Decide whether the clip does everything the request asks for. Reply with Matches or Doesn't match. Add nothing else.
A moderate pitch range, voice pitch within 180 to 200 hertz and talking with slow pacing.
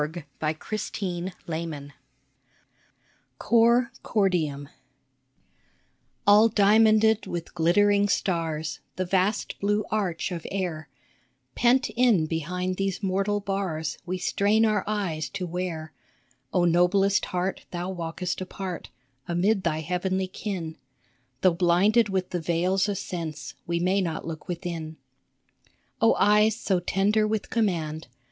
Matches